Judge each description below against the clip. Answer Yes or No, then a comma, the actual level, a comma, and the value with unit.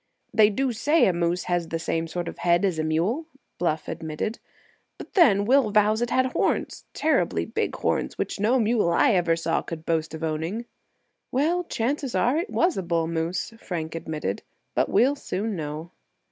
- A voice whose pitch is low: No, medium, 185 Hz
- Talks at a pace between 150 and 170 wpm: No, average, 180 wpm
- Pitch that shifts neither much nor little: No, wide, 6.5 semitones